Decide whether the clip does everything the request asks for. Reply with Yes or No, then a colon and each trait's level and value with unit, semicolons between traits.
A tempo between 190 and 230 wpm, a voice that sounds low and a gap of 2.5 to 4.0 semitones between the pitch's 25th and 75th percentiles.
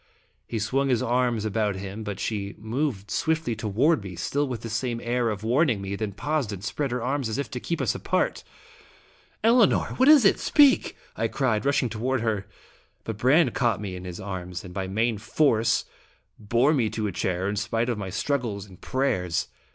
No: average, 200 wpm; low, 115 Hz; average, 4.7 semitones